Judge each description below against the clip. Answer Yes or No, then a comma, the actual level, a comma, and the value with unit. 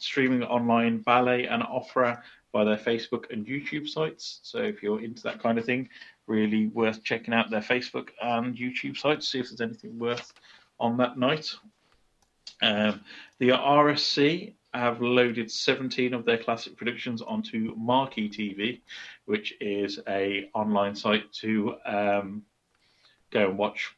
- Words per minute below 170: Yes, average, 150 wpm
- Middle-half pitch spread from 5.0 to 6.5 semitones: No, average, 2.7 semitones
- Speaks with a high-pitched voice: No, low, 120 Hz